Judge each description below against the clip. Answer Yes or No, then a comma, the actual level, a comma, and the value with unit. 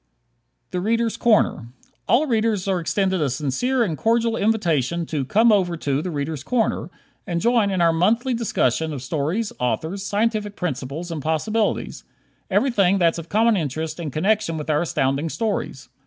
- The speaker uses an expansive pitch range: Yes, wide, 6.1 semitones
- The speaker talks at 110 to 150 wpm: No, average, 160 wpm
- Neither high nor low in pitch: Yes, medium, 180 Hz